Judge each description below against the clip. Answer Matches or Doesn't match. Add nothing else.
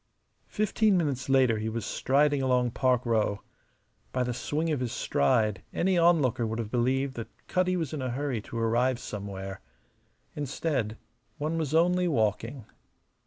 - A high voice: Doesn't match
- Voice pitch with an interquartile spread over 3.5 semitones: Matches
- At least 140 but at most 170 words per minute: Matches